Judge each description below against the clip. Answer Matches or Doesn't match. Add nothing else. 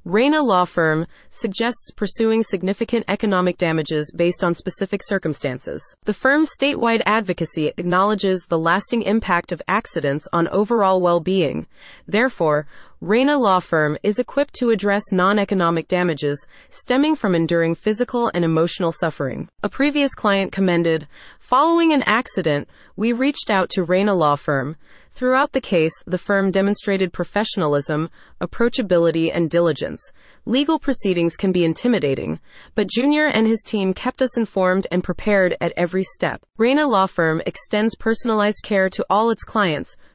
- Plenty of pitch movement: Doesn't match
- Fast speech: Doesn't match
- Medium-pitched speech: Doesn't match